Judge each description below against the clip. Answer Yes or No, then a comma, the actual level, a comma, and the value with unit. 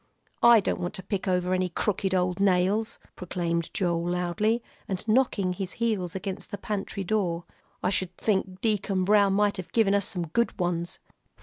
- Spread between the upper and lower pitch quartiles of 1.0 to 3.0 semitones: Yes, narrow, 2.6 semitones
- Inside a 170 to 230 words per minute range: Yes, average, 175 wpm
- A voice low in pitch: No, high, 190 Hz